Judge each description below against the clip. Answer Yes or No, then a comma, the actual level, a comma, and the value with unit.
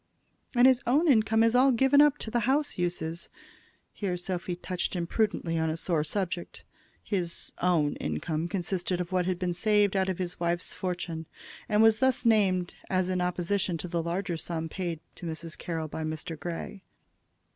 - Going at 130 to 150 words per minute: No, average, 180 wpm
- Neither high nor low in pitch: Yes, medium, 180 Hz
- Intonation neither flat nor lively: Yes, average, 3.7 semitones